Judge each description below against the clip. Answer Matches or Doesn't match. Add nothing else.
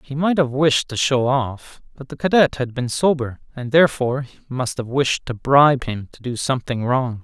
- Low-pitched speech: Matches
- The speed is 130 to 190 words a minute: Doesn't match